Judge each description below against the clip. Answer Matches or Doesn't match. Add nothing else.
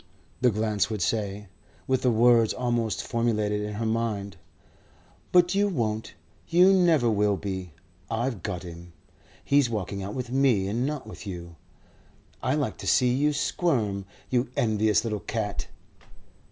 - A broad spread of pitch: Doesn't match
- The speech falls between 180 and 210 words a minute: Doesn't match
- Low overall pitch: Matches